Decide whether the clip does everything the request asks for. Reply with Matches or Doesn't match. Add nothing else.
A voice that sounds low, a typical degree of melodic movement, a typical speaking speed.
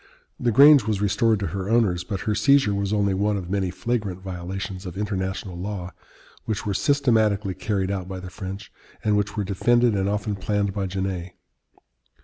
Doesn't match